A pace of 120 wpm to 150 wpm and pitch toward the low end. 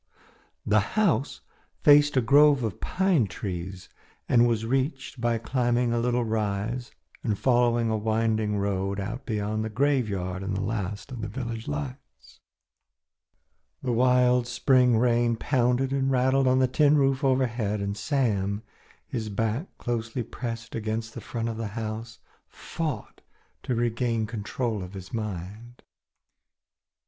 Yes: average, 140 wpm; low, 115 Hz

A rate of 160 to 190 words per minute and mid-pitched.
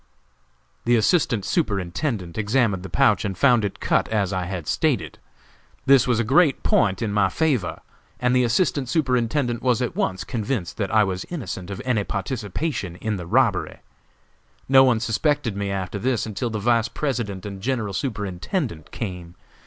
No: average, 165 wpm; low, 110 Hz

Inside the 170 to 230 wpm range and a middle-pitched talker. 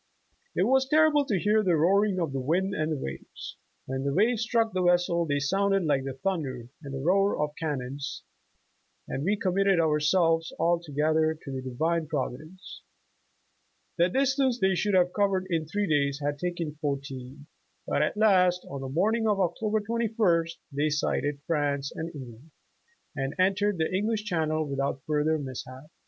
Yes: average, 175 wpm; medium, 165 Hz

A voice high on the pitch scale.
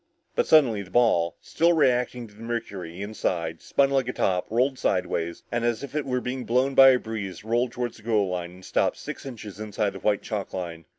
No: low, 115 Hz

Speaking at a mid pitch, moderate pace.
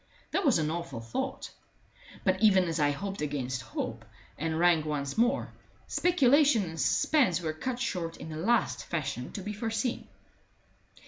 Yes: medium, 175 Hz; average, 155 wpm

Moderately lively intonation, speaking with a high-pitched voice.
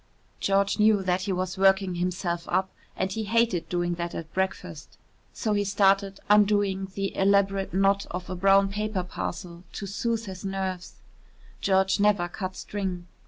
No: narrow, 1.6 semitones; high, 195 Hz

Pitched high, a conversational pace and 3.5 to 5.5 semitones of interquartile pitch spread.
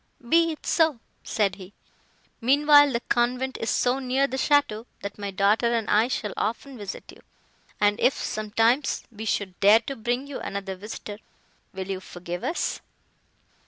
Yes: high, 225 Hz; average, 160 wpm; average, 4.5 semitones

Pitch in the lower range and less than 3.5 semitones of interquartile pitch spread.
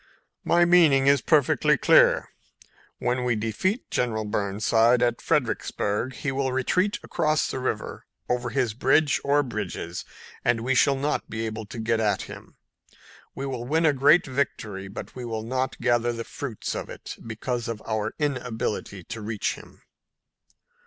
No: low, 120 Hz; average, 3.8 semitones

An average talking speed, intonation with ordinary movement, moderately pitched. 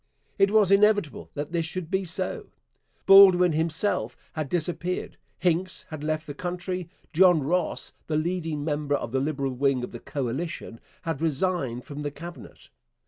Yes: average, 155 wpm; average, 3.8 semitones; medium, 160 Hz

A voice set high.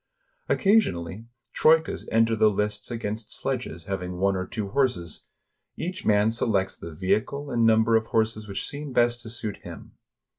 No: low, 110 Hz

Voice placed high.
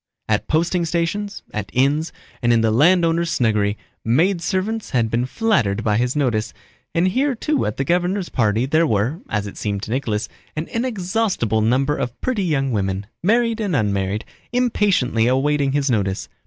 No: medium, 140 Hz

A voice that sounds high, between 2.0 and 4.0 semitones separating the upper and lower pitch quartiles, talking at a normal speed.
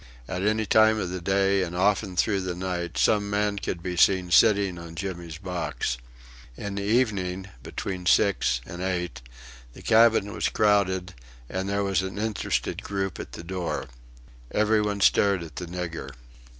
No: very low, 95 Hz; narrow, 2.5 semitones; average, 165 wpm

